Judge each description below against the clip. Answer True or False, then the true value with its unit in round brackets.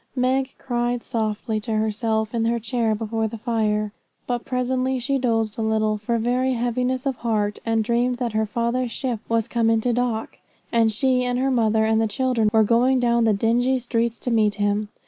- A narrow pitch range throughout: True (2.2 semitones)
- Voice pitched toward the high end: True (230 Hz)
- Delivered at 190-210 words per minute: True (195 wpm)